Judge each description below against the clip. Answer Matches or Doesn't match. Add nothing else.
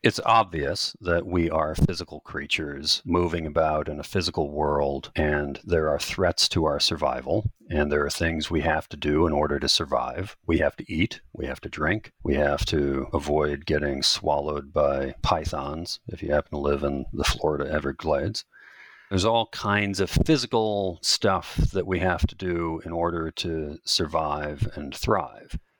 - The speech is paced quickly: Doesn't match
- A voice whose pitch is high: Doesn't match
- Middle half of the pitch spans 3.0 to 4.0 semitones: Matches